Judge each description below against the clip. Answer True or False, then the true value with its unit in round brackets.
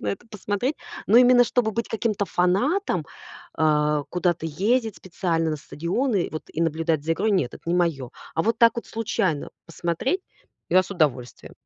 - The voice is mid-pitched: True (180 Hz)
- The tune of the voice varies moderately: False (6.1 semitones)